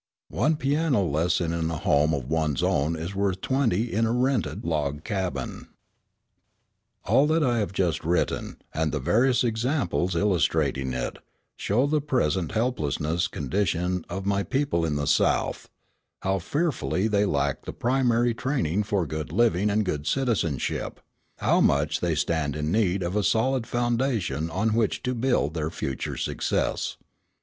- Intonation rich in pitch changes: Yes, wide, 7.1 semitones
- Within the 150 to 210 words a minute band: Yes, average, 155 wpm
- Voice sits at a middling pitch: No, very low, 95 Hz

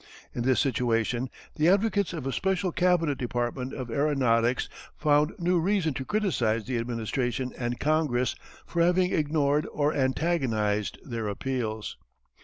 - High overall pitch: No, low, 135 Hz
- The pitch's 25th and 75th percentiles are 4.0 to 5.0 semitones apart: No, wide, 5.5 semitones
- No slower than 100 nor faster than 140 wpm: Yes, slow, 135 wpm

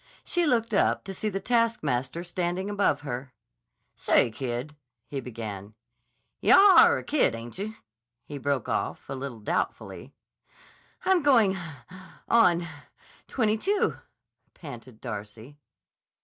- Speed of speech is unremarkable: No, slow, 110 wpm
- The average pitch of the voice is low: No, medium, 155 Hz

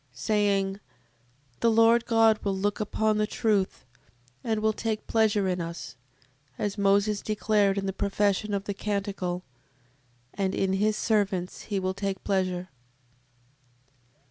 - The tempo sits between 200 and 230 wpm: No, slow, 135 wpm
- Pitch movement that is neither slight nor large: No, narrow, 1.8 semitones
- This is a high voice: Yes, high, 200 Hz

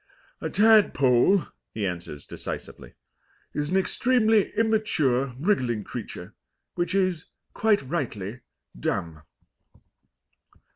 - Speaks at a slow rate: Yes, slow, 90 wpm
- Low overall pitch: No, medium, 160 Hz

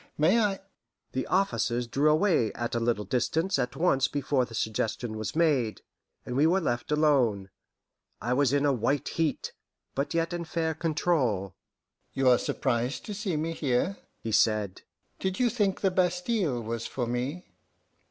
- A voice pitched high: No, medium, 140 Hz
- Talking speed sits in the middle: Yes, average, 170 wpm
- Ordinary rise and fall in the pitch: No, wide, 6.0 semitones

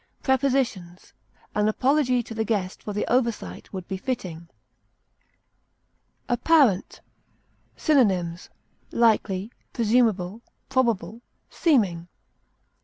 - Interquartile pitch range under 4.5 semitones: No, average, 5.2 semitones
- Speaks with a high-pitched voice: Yes, high, 220 Hz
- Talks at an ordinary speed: No, slow, 85 wpm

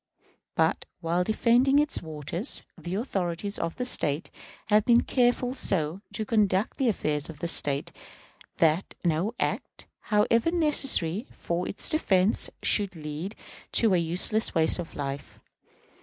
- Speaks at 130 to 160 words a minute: Yes, average, 140 wpm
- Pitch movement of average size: No, wide, 6.0 semitones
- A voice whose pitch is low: No, high, 190 Hz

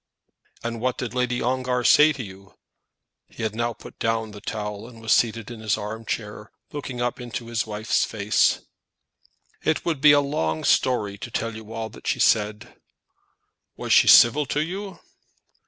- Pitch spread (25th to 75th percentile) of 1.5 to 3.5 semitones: Yes, average, 2.8 semitones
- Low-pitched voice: Yes, low, 115 Hz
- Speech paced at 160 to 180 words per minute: Yes, average, 175 wpm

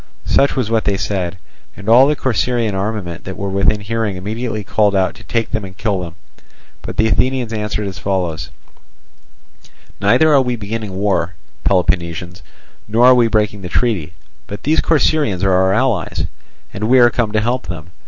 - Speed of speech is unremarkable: Yes, average, 180 wpm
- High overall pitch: No, low, 105 Hz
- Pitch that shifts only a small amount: No, average, 3.7 semitones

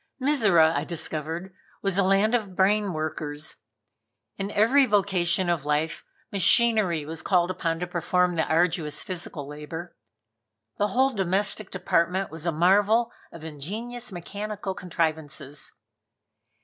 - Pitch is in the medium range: Yes, medium, 180 Hz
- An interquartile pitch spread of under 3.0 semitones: No, average, 4.1 semitones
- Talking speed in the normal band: No, slow, 125 wpm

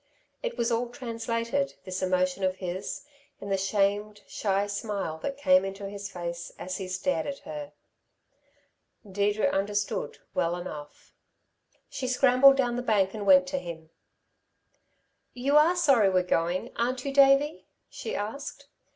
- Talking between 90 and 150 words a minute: Yes, average, 145 wpm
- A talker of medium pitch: No, high, 210 Hz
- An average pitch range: No, wide, 6.4 semitones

